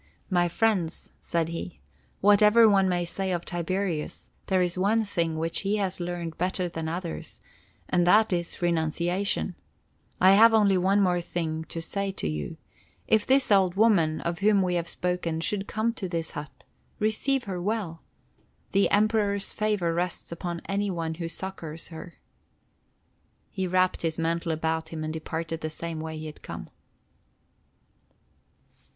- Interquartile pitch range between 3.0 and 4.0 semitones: Yes, average, 3.3 semitones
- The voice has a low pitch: No, medium, 180 Hz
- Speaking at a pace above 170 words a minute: No, average, 155 wpm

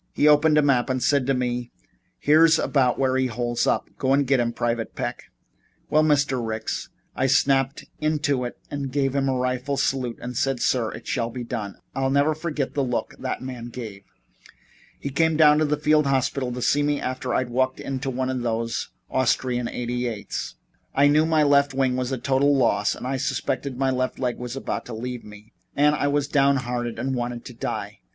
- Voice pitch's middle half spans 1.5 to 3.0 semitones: Yes, narrow, 2.5 semitones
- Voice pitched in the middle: No, low, 130 Hz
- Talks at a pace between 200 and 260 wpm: Yes, fast, 205 wpm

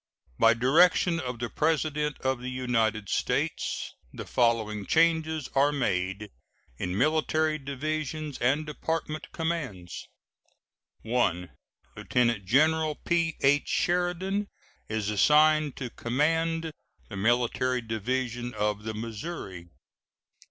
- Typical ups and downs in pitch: No, wide, 5.7 semitones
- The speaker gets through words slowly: Yes, slow, 100 wpm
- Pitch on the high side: No, low, 130 Hz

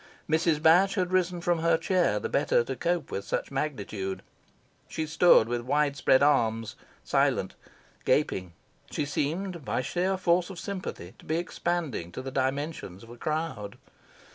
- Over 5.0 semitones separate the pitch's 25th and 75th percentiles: Yes, wide, 5.5 semitones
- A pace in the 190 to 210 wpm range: No, average, 160 wpm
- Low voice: No, medium, 155 Hz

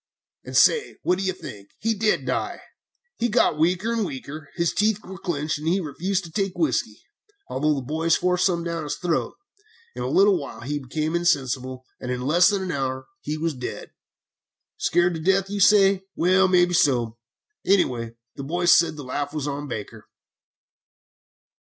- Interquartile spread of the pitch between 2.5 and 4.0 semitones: No, average, 5.0 semitones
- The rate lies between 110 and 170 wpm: No, average, 180 wpm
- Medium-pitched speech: Yes, medium, 165 Hz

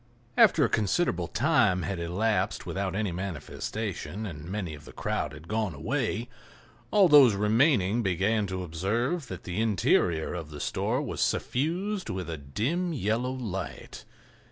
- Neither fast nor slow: Yes, average, 150 wpm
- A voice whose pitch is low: Yes, low, 100 Hz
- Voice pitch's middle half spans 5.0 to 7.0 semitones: Yes, wide, 5.5 semitones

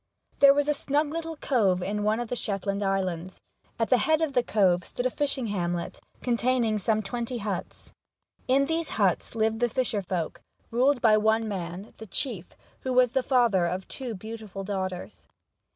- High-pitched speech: Yes, high, 220 Hz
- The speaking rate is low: No, average, 180 wpm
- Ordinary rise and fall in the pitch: Yes, average, 4.7 semitones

